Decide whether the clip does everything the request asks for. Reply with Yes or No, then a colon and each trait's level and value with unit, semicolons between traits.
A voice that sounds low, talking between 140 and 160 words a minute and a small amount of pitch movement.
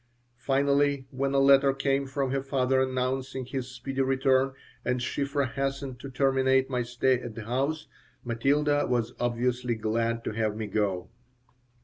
Yes: low, 130 Hz; average, 150 wpm; narrow, 2.1 semitones